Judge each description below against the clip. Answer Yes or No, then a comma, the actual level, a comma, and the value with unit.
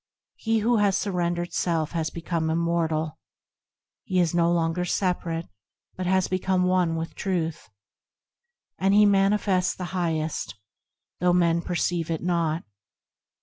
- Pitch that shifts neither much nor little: No, narrow, 2.0 semitones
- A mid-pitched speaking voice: Yes, medium, 175 Hz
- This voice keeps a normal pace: No, slow, 130 wpm